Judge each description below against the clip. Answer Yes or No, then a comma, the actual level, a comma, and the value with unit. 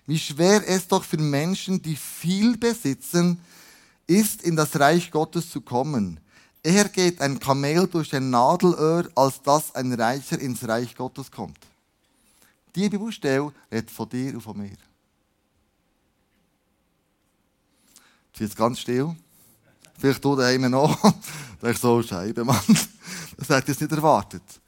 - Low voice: No, medium, 145 Hz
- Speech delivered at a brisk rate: No, average, 140 wpm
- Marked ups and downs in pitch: Yes, wide, 6.1 semitones